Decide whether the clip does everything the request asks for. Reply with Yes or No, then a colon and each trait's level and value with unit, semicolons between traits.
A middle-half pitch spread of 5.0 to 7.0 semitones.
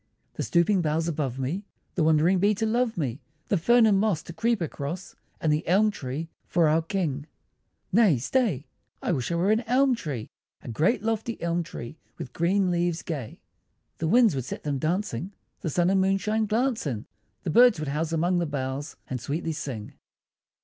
Yes: wide, 5.6 semitones